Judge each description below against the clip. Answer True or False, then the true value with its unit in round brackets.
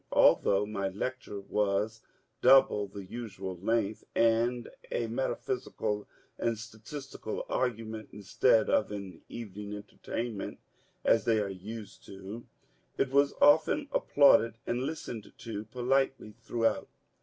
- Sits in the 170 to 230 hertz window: False (110 Hz)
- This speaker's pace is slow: True (115 wpm)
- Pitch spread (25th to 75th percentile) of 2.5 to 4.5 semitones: True (2.9 semitones)